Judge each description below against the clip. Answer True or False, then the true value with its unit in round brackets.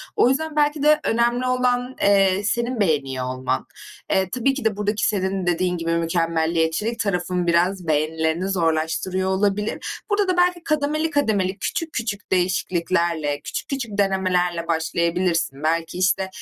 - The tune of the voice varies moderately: False (5.9 semitones)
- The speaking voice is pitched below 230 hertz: True (190 Hz)